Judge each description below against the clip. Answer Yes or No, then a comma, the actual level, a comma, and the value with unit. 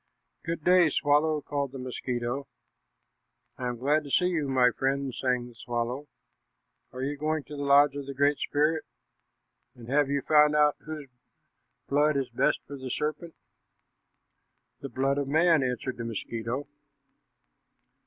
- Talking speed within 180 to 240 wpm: No, average, 155 wpm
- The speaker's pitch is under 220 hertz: Yes, medium, 140 Hz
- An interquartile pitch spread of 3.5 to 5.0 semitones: No, average, 2.7 semitones